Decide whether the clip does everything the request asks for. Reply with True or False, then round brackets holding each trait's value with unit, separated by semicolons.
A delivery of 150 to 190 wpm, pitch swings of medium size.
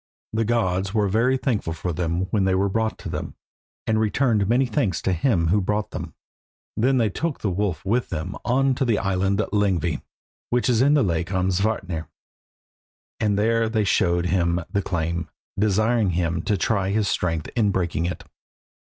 True (180 wpm; 3.8 semitones)